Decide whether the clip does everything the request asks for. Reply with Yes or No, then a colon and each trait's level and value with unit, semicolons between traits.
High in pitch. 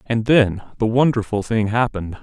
No: low, 115 Hz